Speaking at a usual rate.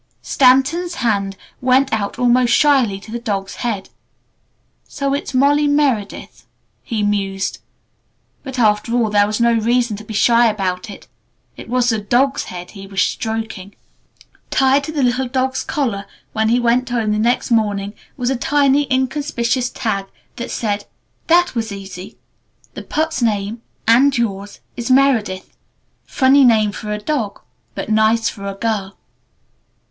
Yes: average, 155 wpm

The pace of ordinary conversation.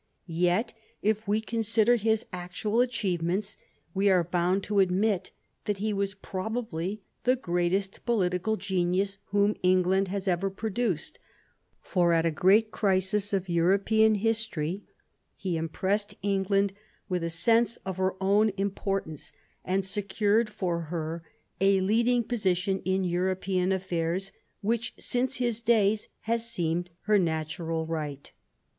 No: slow, 130 wpm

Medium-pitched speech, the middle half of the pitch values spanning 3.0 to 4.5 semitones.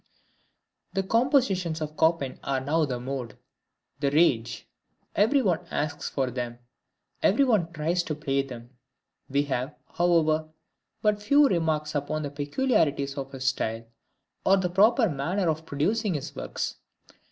No: medium, 155 Hz; wide, 5.4 semitones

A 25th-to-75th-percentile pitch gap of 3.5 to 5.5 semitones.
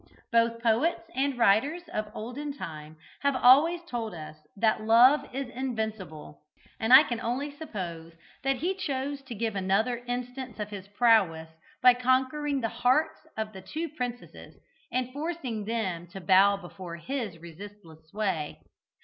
Yes: average, 5.1 semitones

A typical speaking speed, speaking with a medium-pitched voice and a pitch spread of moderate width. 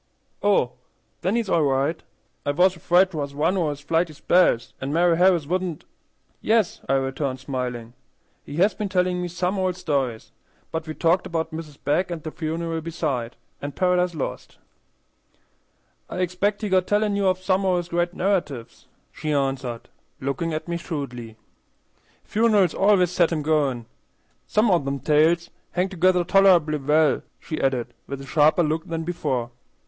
Yes: average, 165 wpm; medium, 165 Hz; average, 4.2 semitones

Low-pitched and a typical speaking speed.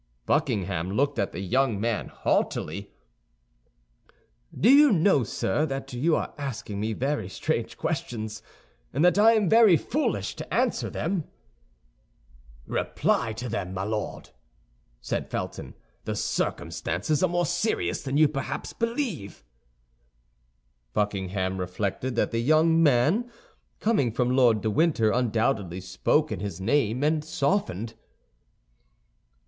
No: low, 125 Hz; slow, 125 wpm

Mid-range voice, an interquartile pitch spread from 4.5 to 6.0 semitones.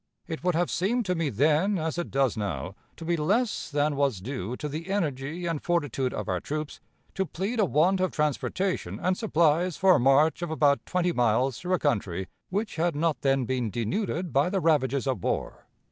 Yes: medium, 155 Hz; average, 5.0 semitones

